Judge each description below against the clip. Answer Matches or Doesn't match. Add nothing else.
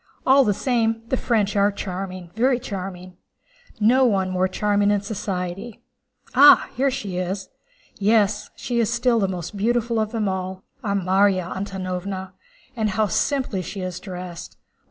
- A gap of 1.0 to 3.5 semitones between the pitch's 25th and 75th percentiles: Matches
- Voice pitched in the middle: Doesn't match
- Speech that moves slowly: Doesn't match